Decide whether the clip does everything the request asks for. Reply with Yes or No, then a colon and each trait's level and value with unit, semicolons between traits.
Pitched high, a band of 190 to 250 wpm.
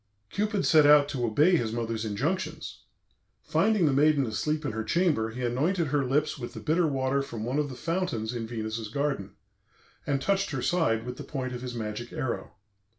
No: low, 135 Hz; average, 195 wpm